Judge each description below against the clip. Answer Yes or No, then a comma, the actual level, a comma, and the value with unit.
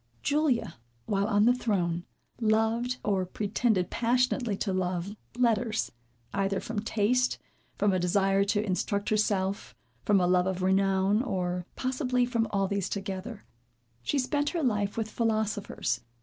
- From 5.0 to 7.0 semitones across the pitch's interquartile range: No, average, 3.4 semitones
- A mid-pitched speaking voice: No, high, 205 Hz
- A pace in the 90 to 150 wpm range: Yes, average, 140 wpm